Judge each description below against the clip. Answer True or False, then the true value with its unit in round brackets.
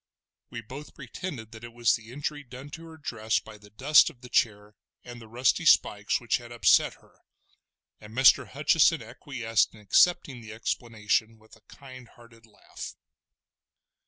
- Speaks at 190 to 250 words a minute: False (165 wpm)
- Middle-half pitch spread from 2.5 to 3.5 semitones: True (2.9 semitones)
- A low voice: True (120 Hz)